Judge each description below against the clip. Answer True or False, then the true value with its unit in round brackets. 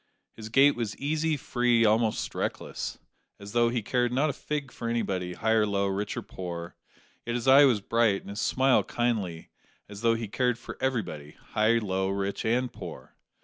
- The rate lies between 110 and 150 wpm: False (190 wpm)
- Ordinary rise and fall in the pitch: True (3.6 semitones)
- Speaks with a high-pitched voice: False (115 Hz)